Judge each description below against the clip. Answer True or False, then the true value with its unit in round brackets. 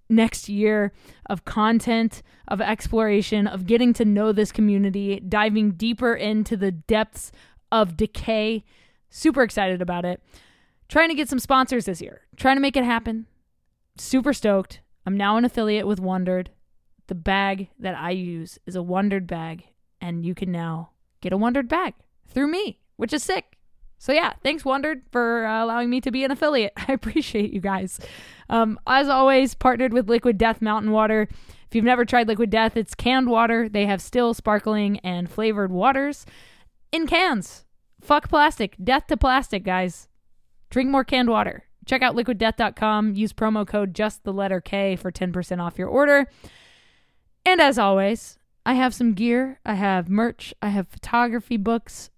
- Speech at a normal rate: True (170 wpm)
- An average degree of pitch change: True (4.1 semitones)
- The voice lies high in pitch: True (220 Hz)